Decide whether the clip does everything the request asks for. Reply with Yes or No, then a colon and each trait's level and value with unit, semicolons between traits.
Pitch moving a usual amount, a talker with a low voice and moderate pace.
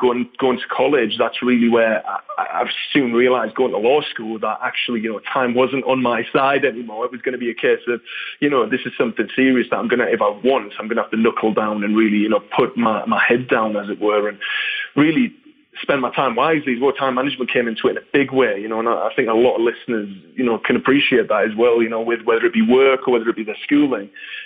No: average, 3.1 semitones; low, 125 Hz; fast, 265 wpm